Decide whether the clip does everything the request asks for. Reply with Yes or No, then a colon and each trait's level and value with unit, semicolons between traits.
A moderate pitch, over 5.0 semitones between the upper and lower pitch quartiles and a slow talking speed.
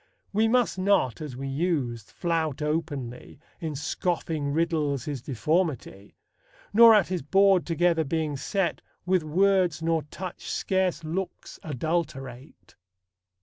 No: medium, 160 Hz; average, 4.3 semitones; slow, 120 wpm